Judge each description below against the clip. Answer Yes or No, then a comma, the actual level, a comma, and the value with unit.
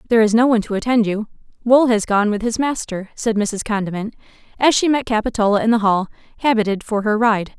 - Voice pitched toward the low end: No, high, 220 Hz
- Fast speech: Yes, fast, 215 wpm